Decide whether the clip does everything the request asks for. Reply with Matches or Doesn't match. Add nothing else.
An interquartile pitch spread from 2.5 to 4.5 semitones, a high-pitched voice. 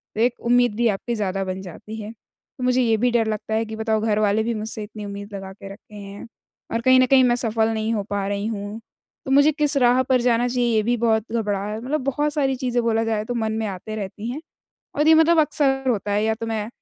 Matches